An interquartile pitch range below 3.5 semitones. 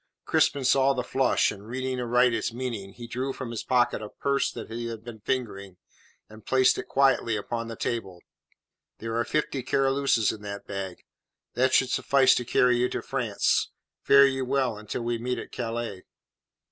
Yes: average, 2.8 semitones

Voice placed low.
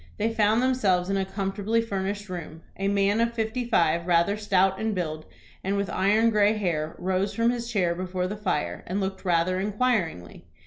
No: high, 195 Hz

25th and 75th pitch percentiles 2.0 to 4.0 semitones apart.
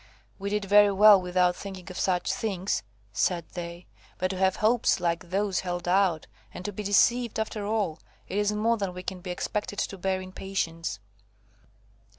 Yes: narrow, 2.5 semitones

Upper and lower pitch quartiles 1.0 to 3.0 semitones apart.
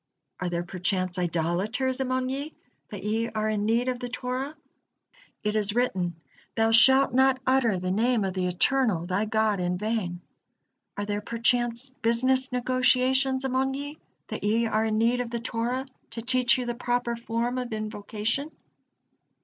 No: average, 3.5 semitones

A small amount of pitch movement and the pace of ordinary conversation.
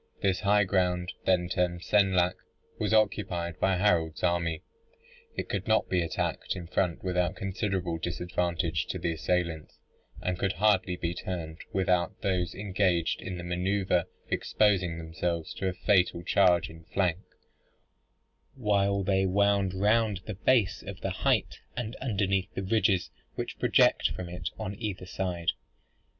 Yes: narrow, 2.1 semitones; average, 145 wpm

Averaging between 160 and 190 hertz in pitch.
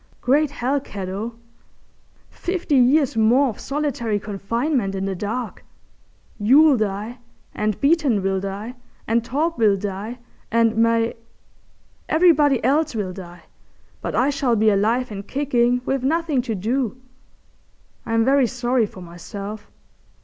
No: high, 235 Hz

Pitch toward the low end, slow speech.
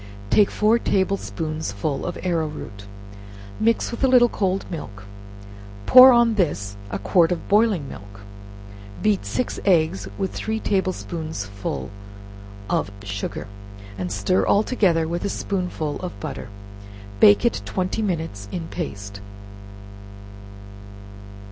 No: medium, 165 Hz; slow, 125 wpm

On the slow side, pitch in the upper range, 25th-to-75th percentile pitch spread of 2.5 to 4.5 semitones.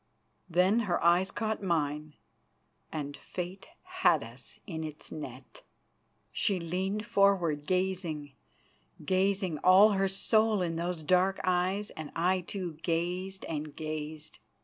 No: slow, 125 wpm; medium, 180 Hz; average, 3.6 semitones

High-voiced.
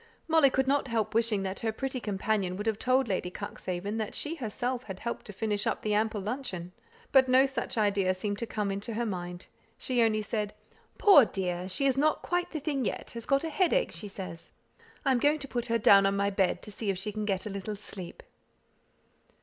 Yes: high, 215 Hz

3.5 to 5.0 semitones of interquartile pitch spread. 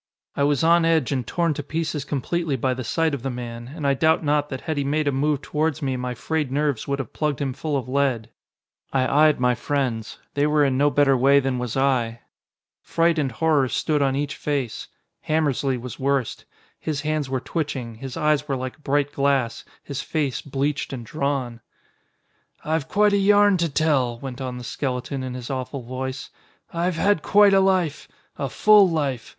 No: average, 3.0 semitones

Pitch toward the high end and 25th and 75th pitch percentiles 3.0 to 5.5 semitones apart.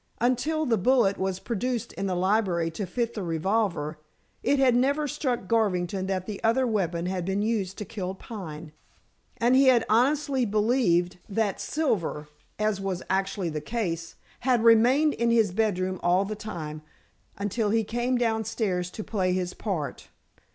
Yes: high, 210 Hz; average, 4.4 semitones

